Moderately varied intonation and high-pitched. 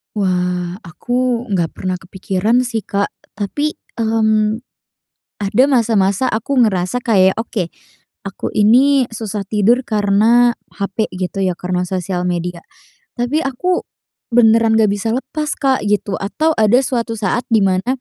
Yes: average, 4.1 semitones; high, 215 Hz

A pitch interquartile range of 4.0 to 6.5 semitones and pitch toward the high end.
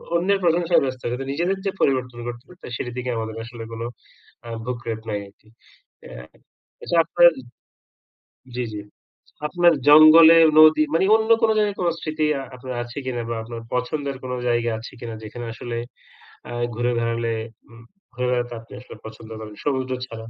No: average, 5.0 semitones; low, 125 Hz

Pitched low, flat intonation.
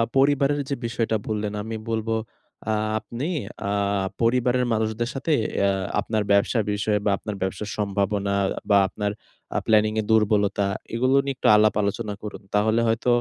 Yes: low, 110 Hz; narrow, 2.2 semitones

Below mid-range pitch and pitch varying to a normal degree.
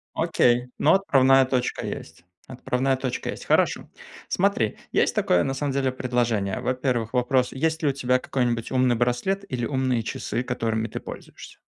No: low, 125 Hz; narrow, 1.8 semitones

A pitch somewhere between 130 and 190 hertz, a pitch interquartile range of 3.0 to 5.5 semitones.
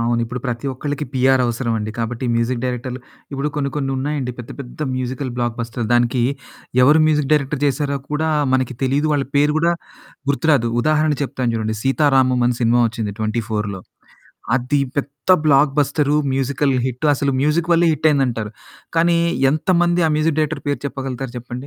Yes: low, 135 Hz; average, 3.4 semitones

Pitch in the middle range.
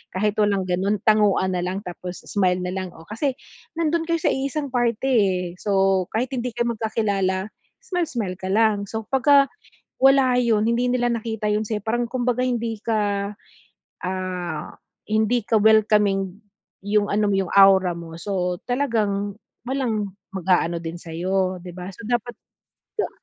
No: high, 210 Hz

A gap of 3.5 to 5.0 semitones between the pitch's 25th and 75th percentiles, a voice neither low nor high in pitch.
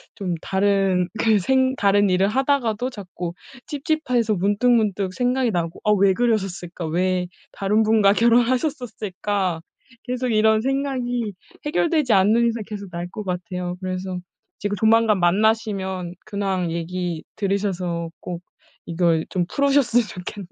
No: average, 4.4 semitones; high, 205 Hz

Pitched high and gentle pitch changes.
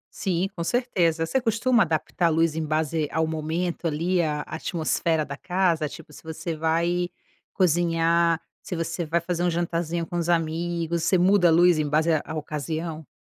No: medium, 165 Hz; narrow, 1.6 semitones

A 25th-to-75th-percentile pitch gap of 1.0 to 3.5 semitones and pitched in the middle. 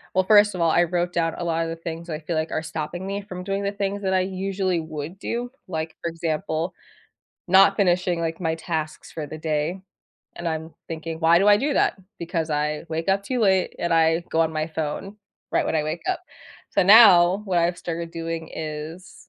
Yes: average, 2.8 semitones; medium, 170 Hz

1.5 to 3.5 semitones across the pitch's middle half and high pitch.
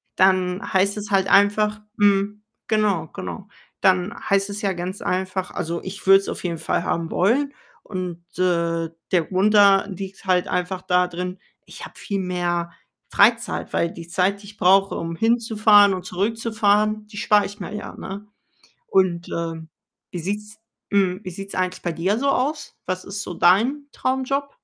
Yes: narrow, 2.5 semitones; high, 195 Hz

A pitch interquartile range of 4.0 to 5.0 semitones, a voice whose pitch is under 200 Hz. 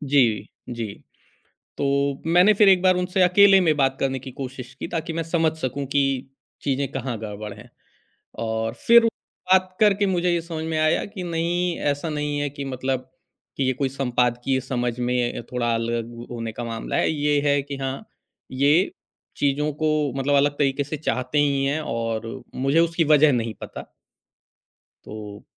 Yes: average, 4.7 semitones; medium, 140 Hz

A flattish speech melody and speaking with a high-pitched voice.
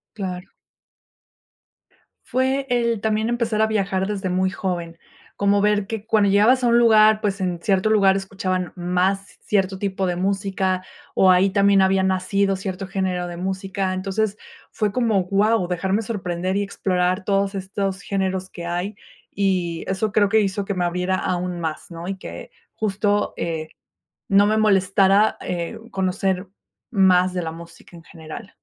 Yes: narrow, 2.0 semitones; high, 195 Hz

